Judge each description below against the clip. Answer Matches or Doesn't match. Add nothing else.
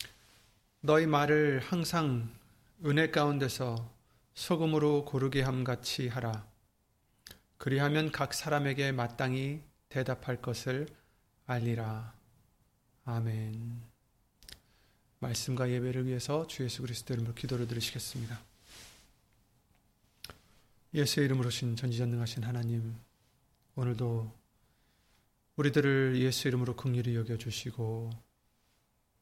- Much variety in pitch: Doesn't match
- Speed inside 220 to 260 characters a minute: Matches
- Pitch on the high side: Doesn't match